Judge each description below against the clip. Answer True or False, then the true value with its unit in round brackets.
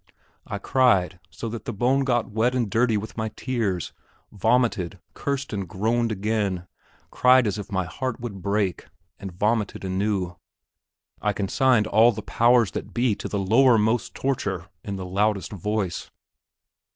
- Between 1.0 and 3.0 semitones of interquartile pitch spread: False (3.6 semitones)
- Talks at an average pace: True (150 wpm)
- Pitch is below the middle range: True (105 Hz)